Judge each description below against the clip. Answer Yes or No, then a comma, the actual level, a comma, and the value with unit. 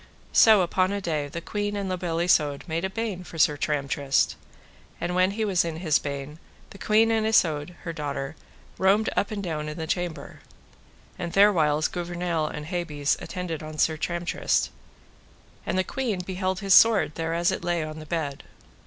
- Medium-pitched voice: Yes, medium, 175 Hz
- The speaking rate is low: No, average, 180 wpm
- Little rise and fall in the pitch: No, average, 3.6 semitones